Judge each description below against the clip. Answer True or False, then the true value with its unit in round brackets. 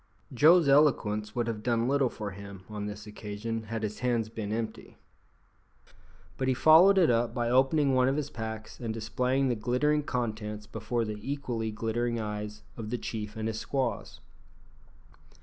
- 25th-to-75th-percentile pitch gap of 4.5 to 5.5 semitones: False (3.3 semitones)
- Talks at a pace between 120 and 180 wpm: True (165 wpm)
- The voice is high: False (115 Hz)